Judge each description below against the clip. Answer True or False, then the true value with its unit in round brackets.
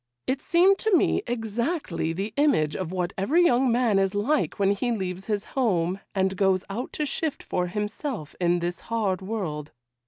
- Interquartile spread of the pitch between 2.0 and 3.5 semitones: False (5.5 semitones)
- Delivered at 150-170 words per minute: False (180 wpm)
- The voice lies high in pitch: True (205 Hz)